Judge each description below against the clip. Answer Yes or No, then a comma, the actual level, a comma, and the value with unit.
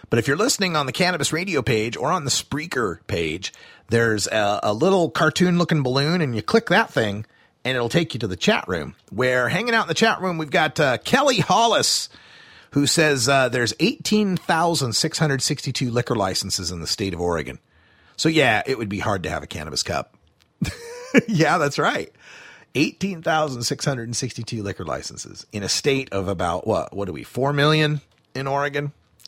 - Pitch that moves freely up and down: Yes, wide, 6.1 semitones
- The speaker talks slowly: No, average, 195 wpm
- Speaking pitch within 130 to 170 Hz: Yes, medium, 140 Hz